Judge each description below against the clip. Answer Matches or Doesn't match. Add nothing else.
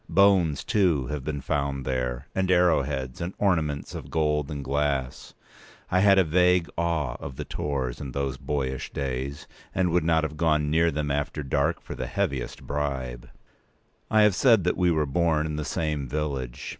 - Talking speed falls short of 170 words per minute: Doesn't match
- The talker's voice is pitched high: Doesn't match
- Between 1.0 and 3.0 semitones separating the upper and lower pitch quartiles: Doesn't match